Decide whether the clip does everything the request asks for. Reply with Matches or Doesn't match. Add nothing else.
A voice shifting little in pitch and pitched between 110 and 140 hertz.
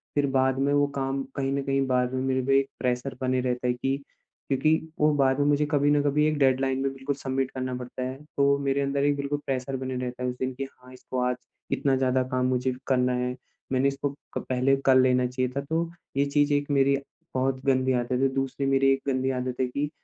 Matches